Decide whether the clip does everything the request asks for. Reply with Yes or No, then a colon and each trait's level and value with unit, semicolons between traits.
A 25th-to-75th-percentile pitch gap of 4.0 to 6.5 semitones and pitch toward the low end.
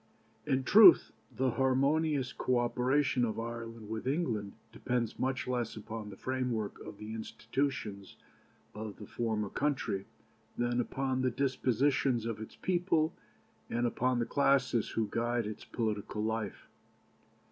No: average, 3.1 semitones; low, 120 Hz